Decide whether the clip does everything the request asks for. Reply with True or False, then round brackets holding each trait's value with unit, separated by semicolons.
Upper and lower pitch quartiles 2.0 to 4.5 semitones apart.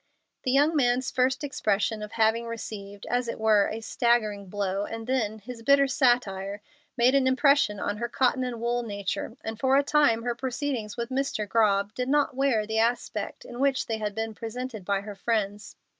True (3.4 semitones)